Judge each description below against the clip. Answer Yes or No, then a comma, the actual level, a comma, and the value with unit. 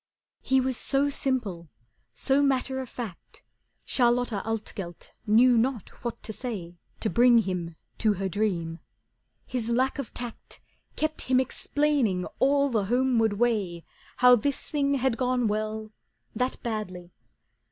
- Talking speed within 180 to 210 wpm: No, slow, 135 wpm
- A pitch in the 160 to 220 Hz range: No, high, 235 Hz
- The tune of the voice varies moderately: Yes, average, 3.9 semitones